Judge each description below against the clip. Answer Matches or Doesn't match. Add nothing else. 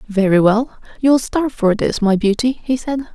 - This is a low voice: Doesn't match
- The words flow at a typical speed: Matches